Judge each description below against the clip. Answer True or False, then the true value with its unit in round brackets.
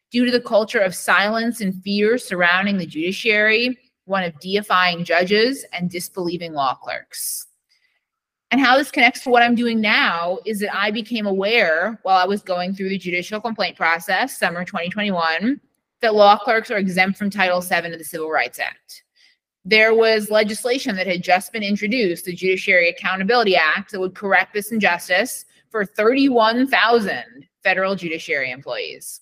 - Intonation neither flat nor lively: True (4.2 semitones)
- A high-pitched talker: True (205 Hz)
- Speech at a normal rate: True (160 wpm)